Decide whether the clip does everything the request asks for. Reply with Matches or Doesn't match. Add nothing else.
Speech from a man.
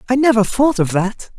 Matches